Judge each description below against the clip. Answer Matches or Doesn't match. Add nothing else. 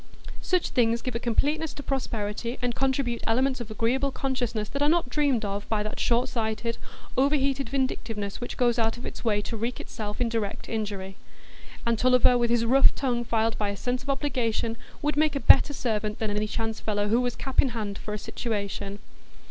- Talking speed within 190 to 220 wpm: Matches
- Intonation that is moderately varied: Matches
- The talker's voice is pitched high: Matches